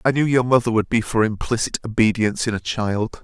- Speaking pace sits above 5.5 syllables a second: Yes, 5.9 syllables/s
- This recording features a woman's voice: No, male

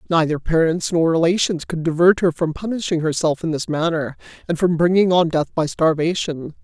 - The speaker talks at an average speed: Yes, average, 180 wpm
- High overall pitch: No, medium, 165 Hz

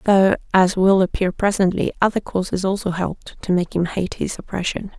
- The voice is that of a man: No, female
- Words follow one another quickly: No, average, 180 wpm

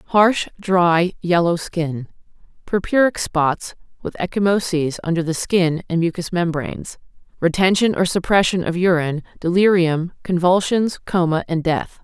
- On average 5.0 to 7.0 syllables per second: No, 4.5 syllables/s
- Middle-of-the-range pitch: Yes, medium, 175 Hz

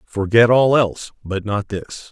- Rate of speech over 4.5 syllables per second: No, 4.3 syllables/s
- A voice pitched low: Yes, low, 110 Hz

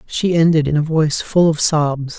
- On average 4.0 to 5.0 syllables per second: Yes, 4.9 syllables/s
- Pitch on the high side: No, medium, 155 Hz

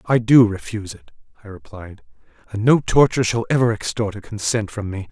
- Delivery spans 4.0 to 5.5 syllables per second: No, 5.8 syllables/s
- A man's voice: Yes, male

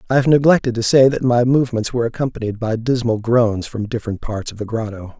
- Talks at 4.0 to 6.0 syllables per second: No, 6.2 syllables/s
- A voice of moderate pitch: No, low, 115 Hz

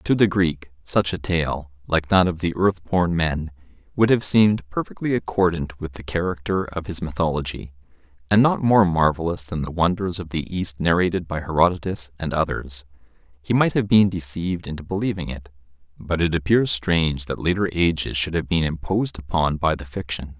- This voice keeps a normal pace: Yes, average, 180 wpm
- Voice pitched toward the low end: Yes, very low, 85 Hz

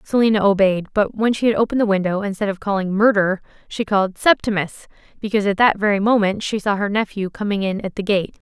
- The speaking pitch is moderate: No, high, 205 Hz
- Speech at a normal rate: No, fast, 210 wpm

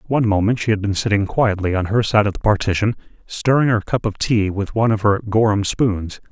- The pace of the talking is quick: Yes, fast, 230 wpm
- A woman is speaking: No, male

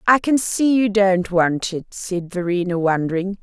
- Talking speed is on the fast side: No, average, 175 wpm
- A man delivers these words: No, female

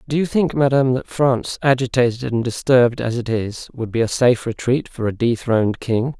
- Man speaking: Yes, male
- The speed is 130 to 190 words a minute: No, fast, 205 wpm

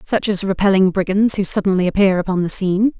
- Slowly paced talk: No, average, 200 wpm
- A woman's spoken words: Yes, female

